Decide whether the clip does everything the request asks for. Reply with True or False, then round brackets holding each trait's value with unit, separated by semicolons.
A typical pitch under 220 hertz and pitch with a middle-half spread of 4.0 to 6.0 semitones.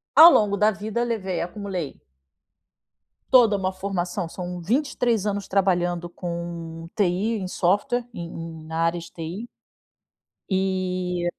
False (185 Hz; 3.2 semitones)